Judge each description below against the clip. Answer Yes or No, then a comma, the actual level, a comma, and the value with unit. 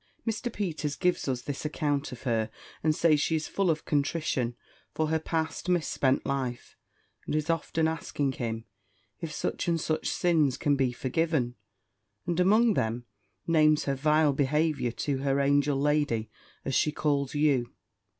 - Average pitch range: Yes, average, 3.0 semitones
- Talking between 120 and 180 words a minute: Yes, average, 160 wpm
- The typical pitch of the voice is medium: Yes, medium, 150 Hz